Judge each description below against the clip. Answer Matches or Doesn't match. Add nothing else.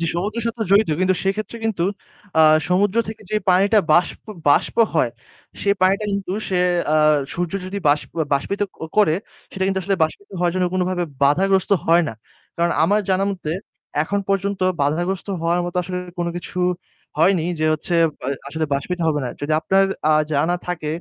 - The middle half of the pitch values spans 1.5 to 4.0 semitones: Matches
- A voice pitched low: Doesn't match